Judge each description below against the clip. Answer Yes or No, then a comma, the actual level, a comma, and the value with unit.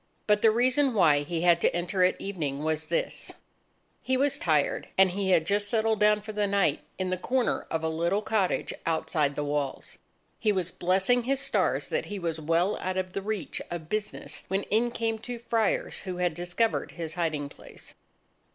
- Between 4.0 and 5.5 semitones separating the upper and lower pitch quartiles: Yes, average, 4.6 semitones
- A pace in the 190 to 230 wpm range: Yes, average, 195 wpm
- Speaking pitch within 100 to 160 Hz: No, high, 190 Hz